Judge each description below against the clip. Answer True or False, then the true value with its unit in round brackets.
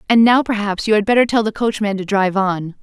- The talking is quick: True (255 wpm)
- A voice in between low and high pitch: False (210 Hz)